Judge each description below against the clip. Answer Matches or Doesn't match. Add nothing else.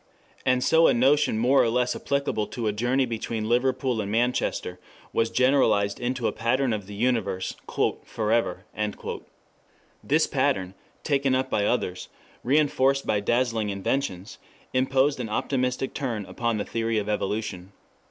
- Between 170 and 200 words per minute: Doesn't match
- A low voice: Matches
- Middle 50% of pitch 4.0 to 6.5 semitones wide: Doesn't match